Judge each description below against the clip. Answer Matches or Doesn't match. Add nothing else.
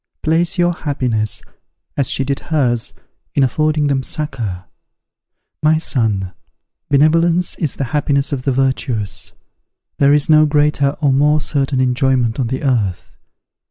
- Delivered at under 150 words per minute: Matches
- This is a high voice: Doesn't match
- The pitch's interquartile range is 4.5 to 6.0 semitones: Doesn't match